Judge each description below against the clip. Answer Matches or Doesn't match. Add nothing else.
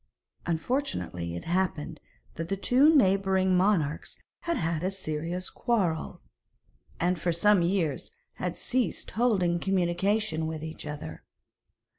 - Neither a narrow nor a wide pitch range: Matches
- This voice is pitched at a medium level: Matches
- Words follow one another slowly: Matches